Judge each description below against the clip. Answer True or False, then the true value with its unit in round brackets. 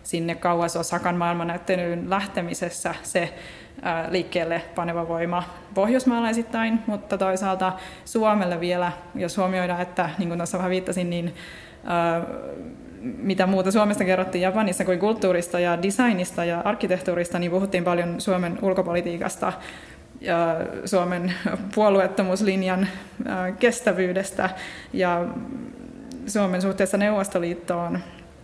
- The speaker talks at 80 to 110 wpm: True (95 wpm)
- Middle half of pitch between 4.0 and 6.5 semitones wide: False (2.6 semitones)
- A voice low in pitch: False (185 Hz)